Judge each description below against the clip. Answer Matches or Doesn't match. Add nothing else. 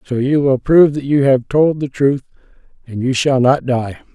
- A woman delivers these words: Doesn't match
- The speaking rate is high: Matches